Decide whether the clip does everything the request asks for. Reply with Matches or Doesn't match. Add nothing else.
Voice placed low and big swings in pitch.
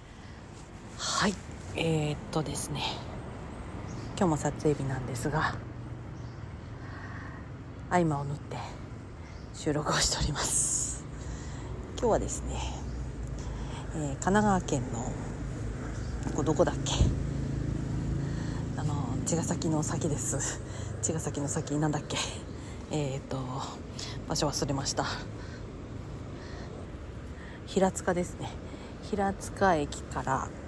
Doesn't match